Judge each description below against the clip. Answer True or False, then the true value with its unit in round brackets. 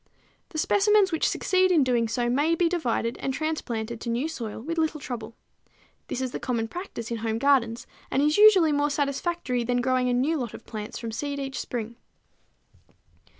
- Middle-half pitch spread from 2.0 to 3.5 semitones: False (5.2 semitones)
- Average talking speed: True (190 wpm)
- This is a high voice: True (260 Hz)